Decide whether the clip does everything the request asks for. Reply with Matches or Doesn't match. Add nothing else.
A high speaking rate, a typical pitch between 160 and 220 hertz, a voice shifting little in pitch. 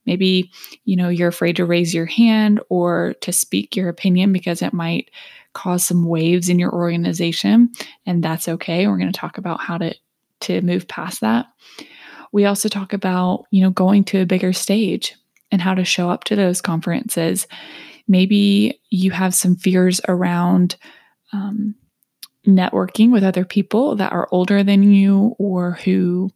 Doesn't match